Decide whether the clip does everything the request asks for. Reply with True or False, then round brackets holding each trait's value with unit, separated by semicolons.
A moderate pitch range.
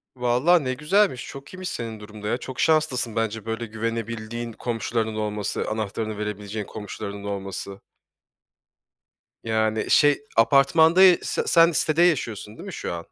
True (4.9 semitones)